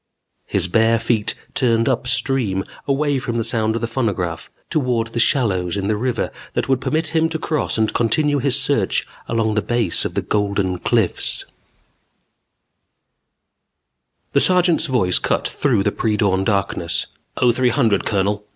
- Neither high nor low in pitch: No, low, 115 Hz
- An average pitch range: Yes, average, 4.4 semitones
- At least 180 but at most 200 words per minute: No, average, 160 wpm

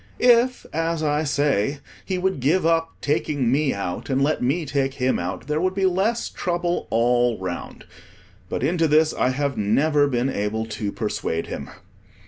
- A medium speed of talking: Yes, average, 170 wpm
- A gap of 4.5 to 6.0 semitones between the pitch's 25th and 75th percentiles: Yes, average, 5.2 semitones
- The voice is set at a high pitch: No, medium, 145 Hz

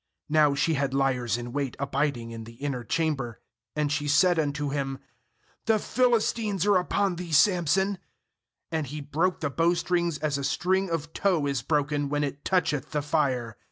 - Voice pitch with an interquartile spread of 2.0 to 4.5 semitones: Yes, average, 4.0 semitones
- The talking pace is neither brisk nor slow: Yes, average, 175 wpm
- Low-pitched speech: No, medium, 150 Hz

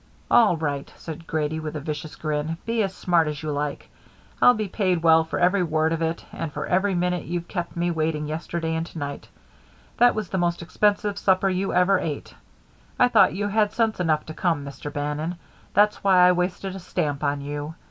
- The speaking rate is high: Yes, fast, 210 wpm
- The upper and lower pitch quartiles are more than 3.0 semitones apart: Yes, average, 3.6 semitones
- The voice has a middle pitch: Yes, medium, 170 Hz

